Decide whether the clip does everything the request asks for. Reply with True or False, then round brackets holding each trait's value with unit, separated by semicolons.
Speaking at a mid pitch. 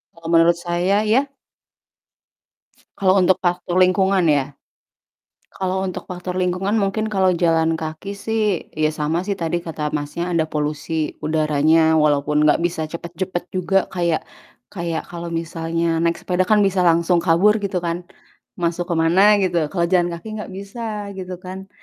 True (175 Hz)